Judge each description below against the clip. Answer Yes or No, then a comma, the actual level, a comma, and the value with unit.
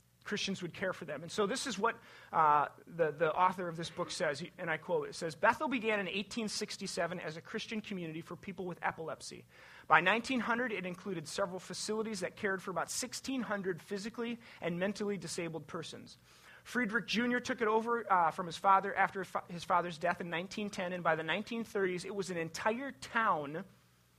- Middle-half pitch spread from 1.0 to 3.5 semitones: No, average, 4.3 semitones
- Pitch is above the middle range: Yes, high, 195 Hz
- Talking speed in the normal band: Yes, average, 190 wpm